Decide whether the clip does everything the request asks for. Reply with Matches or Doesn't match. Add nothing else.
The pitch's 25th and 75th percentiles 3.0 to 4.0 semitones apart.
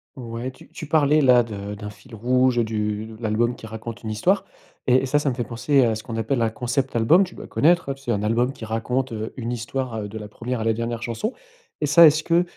Matches